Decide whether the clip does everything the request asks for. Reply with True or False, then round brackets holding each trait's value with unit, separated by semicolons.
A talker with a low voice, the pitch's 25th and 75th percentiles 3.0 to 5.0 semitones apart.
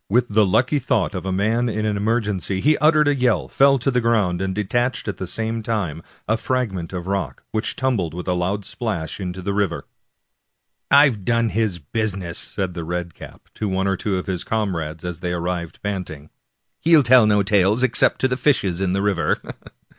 True (100 Hz; 4.4 semitones)